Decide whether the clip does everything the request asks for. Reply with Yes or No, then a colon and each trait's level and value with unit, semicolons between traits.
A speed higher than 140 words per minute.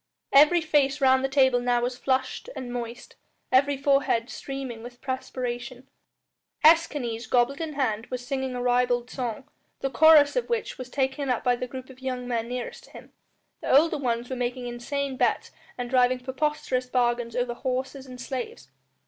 Yes: average, 175 wpm